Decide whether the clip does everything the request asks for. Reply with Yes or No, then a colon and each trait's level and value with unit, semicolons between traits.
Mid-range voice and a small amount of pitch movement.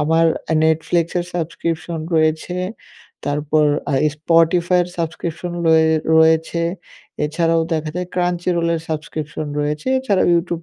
Yes: medium, 165 Hz; narrow, 1.5 semitones